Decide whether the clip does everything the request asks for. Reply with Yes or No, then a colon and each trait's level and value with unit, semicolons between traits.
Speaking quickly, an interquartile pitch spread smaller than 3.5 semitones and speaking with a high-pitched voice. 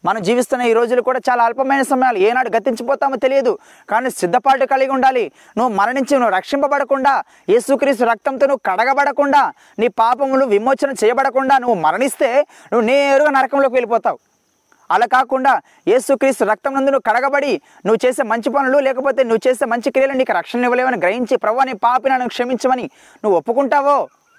Yes: fast, 140 wpm; narrow, 2.4 semitones; very high, 265 Hz